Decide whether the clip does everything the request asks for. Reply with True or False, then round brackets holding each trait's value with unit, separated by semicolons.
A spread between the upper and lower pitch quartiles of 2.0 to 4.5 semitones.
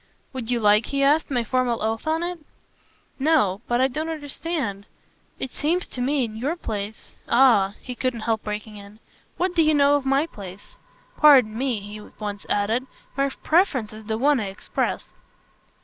False (5.2 semitones)